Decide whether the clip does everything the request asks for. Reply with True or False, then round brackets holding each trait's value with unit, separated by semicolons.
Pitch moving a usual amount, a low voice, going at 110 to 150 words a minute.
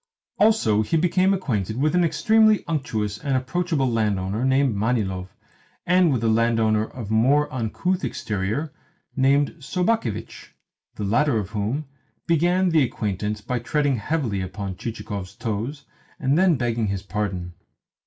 False (6.4 semitones; 120 Hz; 135 wpm)